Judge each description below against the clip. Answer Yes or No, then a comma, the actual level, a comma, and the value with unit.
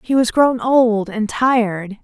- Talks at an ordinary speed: Yes, average, 175 wpm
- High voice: Yes, high, 230 Hz